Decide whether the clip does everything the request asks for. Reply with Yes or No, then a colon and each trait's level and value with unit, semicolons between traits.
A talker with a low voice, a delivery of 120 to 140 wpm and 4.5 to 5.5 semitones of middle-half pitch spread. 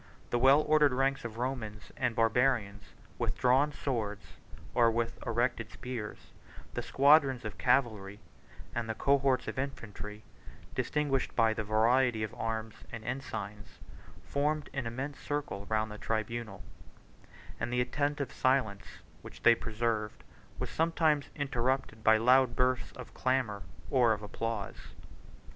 No: low, 120 Hz; slow, 135 wpm; average, 3.6 semitones